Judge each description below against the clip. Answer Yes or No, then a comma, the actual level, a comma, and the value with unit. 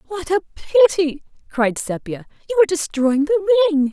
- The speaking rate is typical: Yes, average, 155 wpm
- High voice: Yes, very high, 280 Hz